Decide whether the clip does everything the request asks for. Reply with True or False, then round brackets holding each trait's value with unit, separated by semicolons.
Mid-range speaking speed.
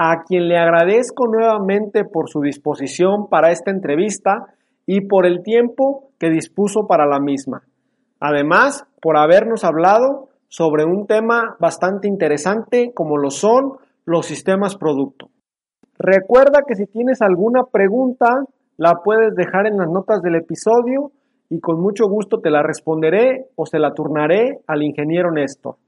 True (145 wpm)